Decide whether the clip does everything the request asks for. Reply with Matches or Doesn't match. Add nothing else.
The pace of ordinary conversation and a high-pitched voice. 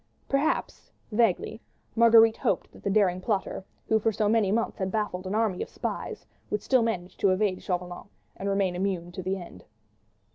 Matches